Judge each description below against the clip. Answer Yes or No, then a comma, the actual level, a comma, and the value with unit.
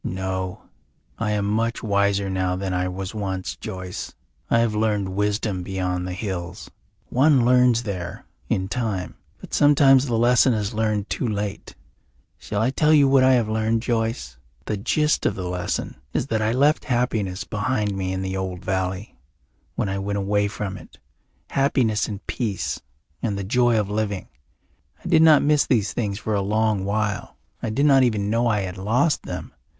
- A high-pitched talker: No, low, 105 Hz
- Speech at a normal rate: Yes, average, 180 wpm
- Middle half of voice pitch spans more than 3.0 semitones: Yes, average, 3.8 semitones